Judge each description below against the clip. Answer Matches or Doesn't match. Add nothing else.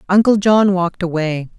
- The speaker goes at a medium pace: Matches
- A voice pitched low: Doesn't match